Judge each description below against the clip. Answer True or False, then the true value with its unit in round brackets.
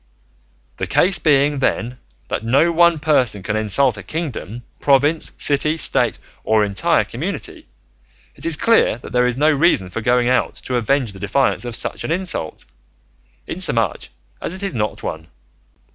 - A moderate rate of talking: True (160 wpm)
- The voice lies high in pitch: False (130 Hz)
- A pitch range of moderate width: False (5.8 semitones)